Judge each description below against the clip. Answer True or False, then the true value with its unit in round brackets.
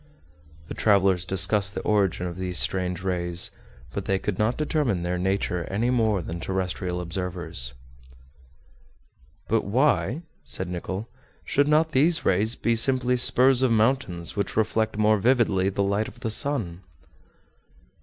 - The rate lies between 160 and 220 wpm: False (145 wpm)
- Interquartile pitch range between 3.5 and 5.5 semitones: True (4.7 semitones)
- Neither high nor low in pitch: False (100 Hz)